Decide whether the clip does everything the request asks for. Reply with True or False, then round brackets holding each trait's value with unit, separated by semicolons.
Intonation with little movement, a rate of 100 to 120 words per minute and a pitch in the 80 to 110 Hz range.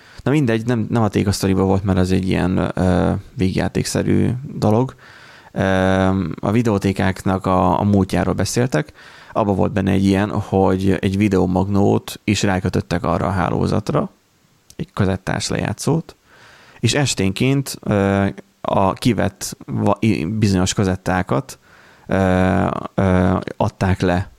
True (2.3 semitones; 110 wpm; 95 Hz)